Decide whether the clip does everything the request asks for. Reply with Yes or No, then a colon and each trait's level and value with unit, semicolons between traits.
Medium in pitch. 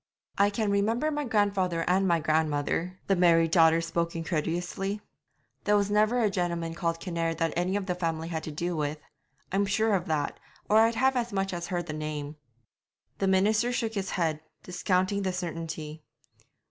Yes: medium, 180 Hz